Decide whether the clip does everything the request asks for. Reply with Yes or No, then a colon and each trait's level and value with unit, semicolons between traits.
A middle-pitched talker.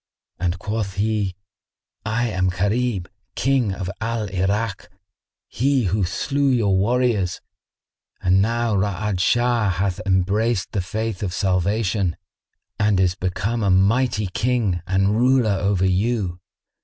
No: low, 100 Hz